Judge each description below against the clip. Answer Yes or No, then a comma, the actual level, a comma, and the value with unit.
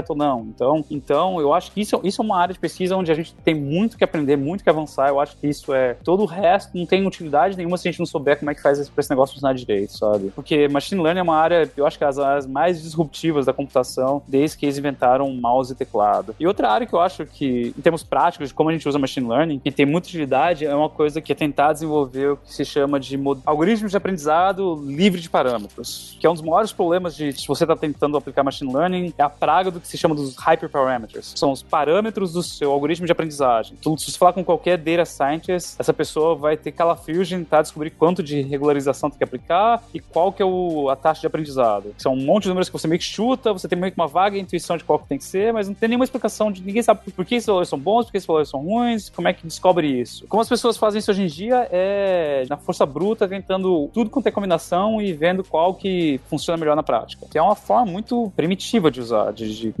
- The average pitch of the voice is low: No, medium, 160 Hz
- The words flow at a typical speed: No, fast, 265 wpm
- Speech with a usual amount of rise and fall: Yes, average, 4.5 semitones